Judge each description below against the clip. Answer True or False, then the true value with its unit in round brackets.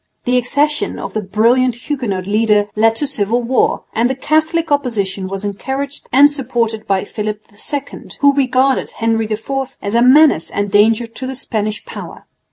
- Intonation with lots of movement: False (4.2 semitones)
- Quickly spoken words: False (170 wpm)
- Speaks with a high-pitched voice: True (235 Hz)